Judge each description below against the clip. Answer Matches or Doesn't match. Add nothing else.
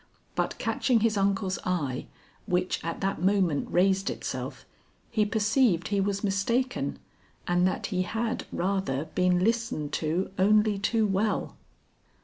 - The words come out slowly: Matches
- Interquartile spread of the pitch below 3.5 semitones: Matches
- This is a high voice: Matches